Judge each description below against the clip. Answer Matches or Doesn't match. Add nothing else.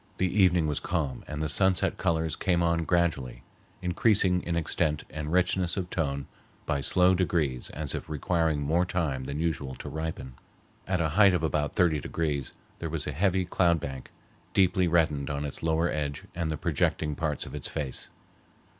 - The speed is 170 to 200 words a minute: Matches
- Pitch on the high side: Doesn't match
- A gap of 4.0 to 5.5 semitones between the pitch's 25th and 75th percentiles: Doesn't match